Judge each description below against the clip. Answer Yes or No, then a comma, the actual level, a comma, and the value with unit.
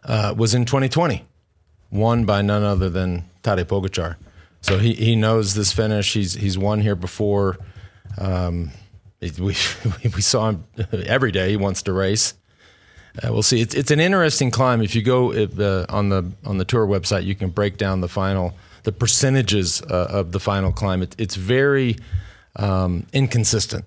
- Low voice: Yes, low, 100 Hz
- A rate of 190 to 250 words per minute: No, average, 175 wpm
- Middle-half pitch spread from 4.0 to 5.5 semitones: No, average, 3.1 semitones